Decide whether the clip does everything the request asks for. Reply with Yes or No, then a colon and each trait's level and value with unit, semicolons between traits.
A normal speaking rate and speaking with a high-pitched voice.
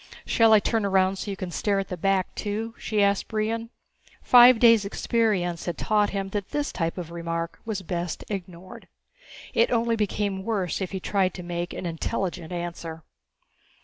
Yes: average, 180 wpm; high, 195 Hz